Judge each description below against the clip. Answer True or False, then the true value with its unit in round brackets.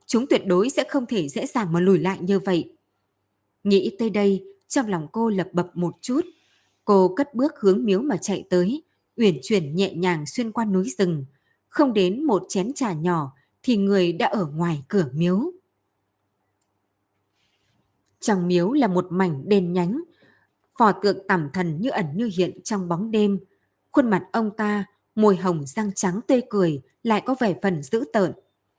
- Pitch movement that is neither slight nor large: True (4.4 semitones)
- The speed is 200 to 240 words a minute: False (180 wpm)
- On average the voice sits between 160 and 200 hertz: True (190 Hz)